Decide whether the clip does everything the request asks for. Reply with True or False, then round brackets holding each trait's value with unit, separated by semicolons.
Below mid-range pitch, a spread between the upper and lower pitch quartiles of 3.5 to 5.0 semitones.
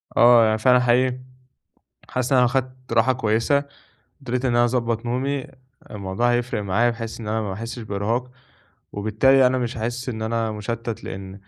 False (120 Hz; 2.4 semitones)